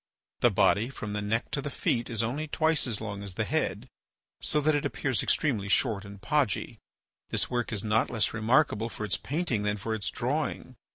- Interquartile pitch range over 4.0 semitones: Yes, average, 4.8 semitones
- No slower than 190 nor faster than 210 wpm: Yes, fast, 205 wpm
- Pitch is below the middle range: Yes, low, 115 Hz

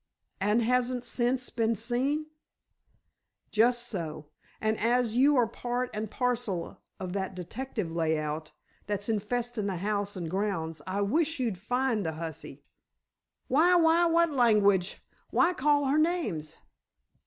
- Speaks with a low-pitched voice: No, high, 225 Hz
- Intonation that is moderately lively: Yes, average, 4.9 semitones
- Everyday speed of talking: No, slow, 130 wpm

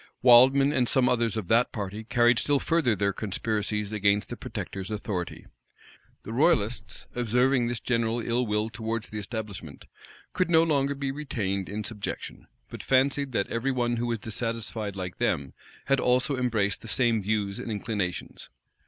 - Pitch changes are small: No, average, 3.2 semitones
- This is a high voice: No, low, 115 Hz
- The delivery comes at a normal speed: Yes, average, 160 wpm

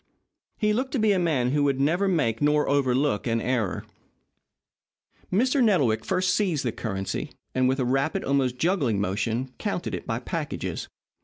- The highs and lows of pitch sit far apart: Yes, wide, 6.8 semitones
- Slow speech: No, average, 165 wpm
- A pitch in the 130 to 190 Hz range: Yes, medium, 140 Hz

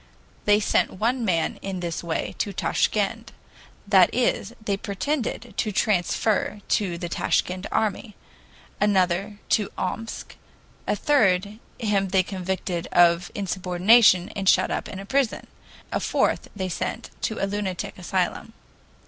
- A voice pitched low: No, high, 195 Hz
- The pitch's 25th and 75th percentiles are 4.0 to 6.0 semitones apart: No, average, 2.8 semitones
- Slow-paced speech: Yes, slow, 130 wpm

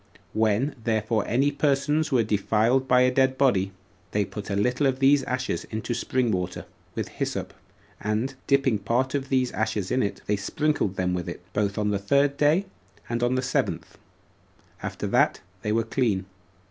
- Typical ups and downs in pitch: Yes, average, 4.3 semitones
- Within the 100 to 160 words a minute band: No, average, 180 wpm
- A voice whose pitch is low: Yes, low, 120 Hz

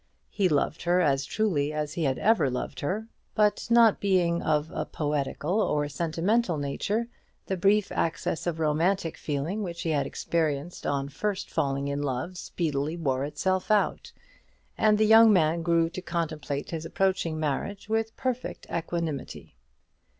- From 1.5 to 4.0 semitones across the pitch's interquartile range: No, average, 5.0 semitones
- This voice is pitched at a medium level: Yes, medium, 165 Hz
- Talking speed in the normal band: Yes, average, 155 wpm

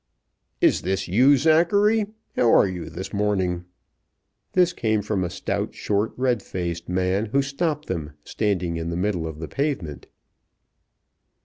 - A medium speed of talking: Yes, average, 145 wpm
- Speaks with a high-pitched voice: No, low, 100 Hz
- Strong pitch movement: Yes, wide, 7.3 semitones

